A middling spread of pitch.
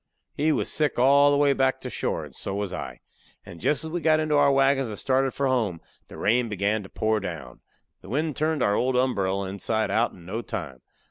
No: wide, 6.0 semitones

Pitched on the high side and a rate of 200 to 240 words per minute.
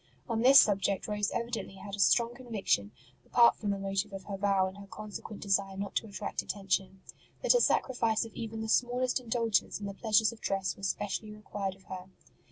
Yes: high, 205 Hz; fast, 205 wpm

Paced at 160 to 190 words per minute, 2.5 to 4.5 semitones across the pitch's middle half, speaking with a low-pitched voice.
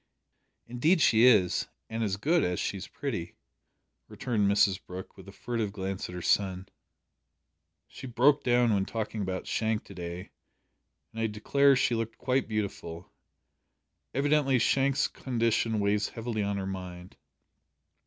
No: average, 145 wpm; average, 4.2 semitones; low, 110 Hz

